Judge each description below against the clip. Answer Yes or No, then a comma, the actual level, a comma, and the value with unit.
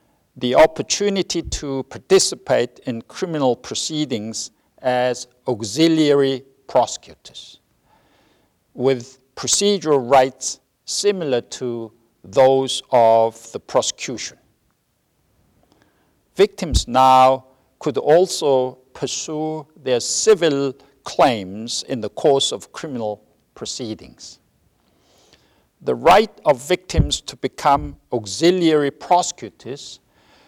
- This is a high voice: No, low, 130 Hz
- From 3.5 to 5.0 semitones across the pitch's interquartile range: Yes, average, 3.9 semitones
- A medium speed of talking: No, slow, 80 wpm